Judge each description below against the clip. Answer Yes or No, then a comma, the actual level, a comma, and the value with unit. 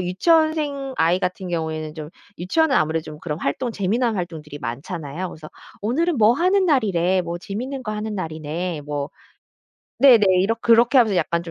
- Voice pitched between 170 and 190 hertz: Yes, medium, 185 Hz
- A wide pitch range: Yes, wide, 7.2 semitones